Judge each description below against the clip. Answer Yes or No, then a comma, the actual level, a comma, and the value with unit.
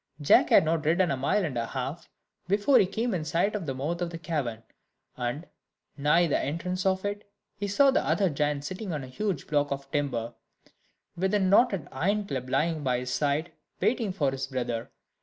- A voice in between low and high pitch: Yes, medium, 160 Hz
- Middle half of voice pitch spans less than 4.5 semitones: No, wide, 5.6 semitones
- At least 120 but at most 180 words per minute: No, average, 200 wpm